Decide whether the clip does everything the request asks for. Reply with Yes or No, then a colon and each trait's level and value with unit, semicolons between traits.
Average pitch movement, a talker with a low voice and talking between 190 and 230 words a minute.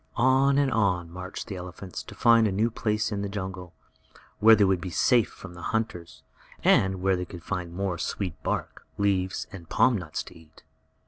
Yes: average, 3.3 semitones; very low, 95 Hz; average, 195 wpm